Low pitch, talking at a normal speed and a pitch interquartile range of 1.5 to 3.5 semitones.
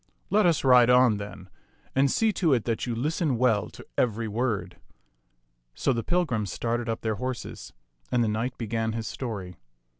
Yes: low, 120 Hz; average, 175 wpm; average, 2.7 semitones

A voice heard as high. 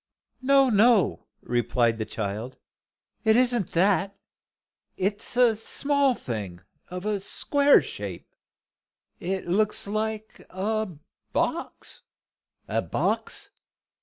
Yes: high, 205 Hz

